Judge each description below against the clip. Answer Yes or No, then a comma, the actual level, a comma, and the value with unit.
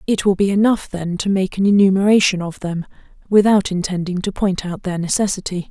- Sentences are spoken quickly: No, average, 190 wpm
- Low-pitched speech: No, high, 190 Hz